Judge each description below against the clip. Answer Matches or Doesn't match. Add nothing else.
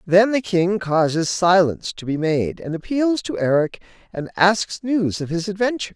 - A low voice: Doesn't match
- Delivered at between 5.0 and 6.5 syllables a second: Doesn't match